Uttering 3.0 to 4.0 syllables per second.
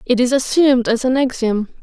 No: 5.6 syllables/s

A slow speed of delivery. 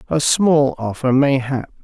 Yes: slow, 130 wpm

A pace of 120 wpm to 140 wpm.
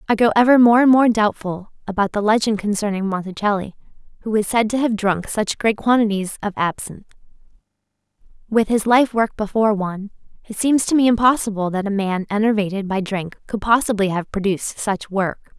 No: average, 175 wpm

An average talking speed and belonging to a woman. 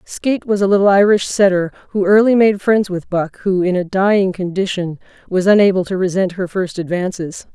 Yes: average, 190 wpm; female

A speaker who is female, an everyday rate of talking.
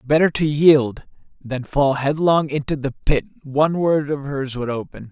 No: male; average, 175 wpm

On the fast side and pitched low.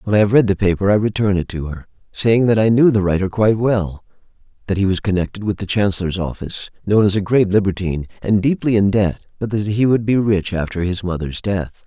Yes: fast, 235 wpm; low, 100 Hz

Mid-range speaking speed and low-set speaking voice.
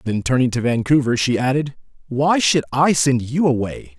Yes: average, 180 wpm; low, 130 Hz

